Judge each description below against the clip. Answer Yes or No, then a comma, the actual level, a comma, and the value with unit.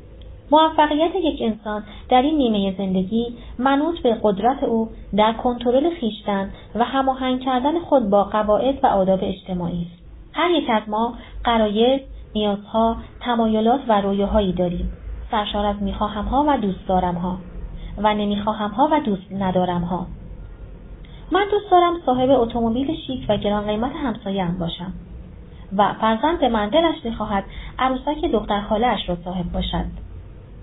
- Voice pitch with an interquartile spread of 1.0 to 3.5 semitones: No, average, 4.7 semitones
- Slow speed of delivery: No, average, 145 wpm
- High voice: Yes, high, 215 Hz